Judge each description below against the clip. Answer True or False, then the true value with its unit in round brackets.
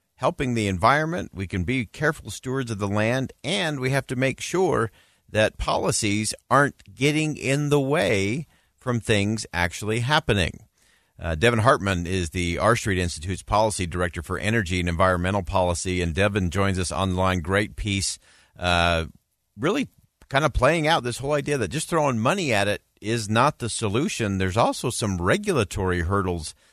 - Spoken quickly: False (165 wpm)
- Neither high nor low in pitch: False (105 Hz)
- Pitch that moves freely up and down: True (5.8 semitones)